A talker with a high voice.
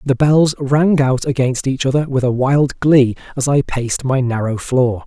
No: low, 135 Hz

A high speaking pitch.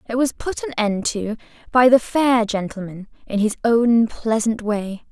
Yes: high, 225 Hz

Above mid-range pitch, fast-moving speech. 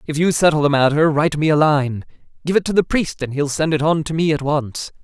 No: medium, 150 Hz; fast, 275 wpm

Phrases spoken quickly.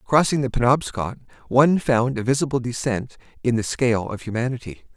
No: average, 155 wpm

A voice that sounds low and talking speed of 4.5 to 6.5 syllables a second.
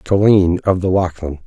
Yes: very low, 90 Hz; 5.0 syllables/s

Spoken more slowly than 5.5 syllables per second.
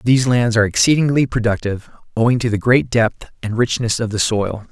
No: 5.9 syllables/s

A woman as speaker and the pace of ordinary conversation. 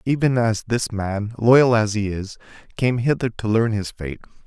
No: male; average, 190 wpm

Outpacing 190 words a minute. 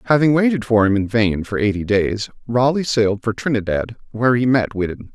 Yes: average, 200 wpm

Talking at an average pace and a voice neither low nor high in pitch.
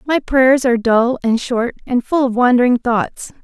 No: average, 190 wpm; high, 245 Hz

